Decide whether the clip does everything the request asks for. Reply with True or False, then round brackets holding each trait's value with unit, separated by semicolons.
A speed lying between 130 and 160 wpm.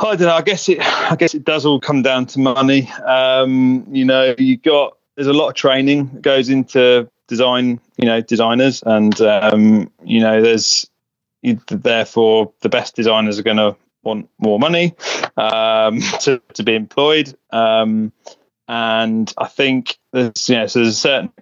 False (175 wpm)